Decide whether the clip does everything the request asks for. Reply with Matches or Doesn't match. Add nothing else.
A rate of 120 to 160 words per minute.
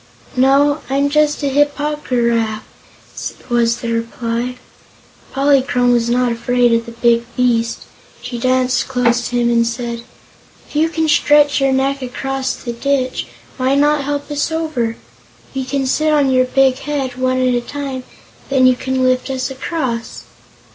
Doesn't match